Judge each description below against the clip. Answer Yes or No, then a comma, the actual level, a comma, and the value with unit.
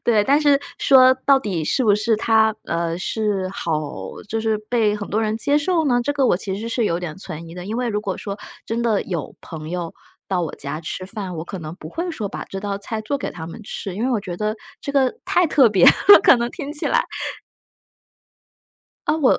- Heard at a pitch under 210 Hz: No, high, 215 Hz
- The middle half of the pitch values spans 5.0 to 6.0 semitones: Yes, average, 5.3 semitones